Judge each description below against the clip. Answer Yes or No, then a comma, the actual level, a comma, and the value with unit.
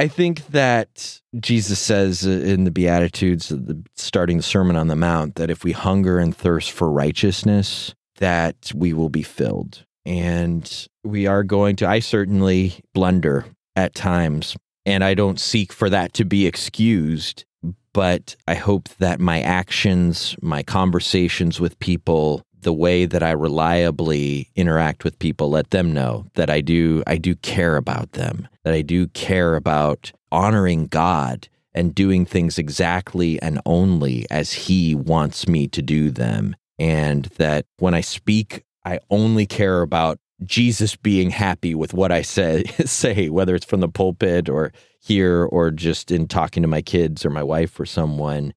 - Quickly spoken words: No, average, 160 wpm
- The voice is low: Yes, very low, 90 Hz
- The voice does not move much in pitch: No, average, 3.3 semitones